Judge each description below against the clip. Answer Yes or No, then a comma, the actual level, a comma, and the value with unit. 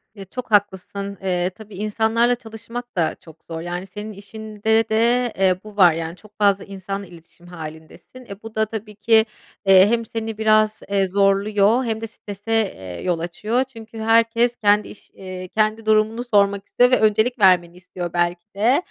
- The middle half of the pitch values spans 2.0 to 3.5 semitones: Yes, average, 3.0 semitones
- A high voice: Yes, high, 210 Hz